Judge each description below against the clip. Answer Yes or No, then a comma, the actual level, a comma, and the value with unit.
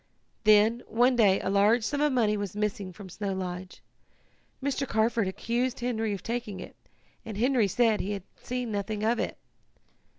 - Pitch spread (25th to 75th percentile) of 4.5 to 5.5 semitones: No, average, 3.2 semitones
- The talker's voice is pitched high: Yes, high, 215 Hz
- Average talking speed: Yes, average, 170 wpm